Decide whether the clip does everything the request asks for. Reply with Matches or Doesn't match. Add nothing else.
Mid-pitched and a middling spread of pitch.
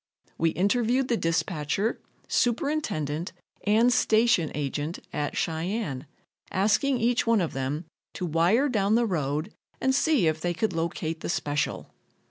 Doesn't match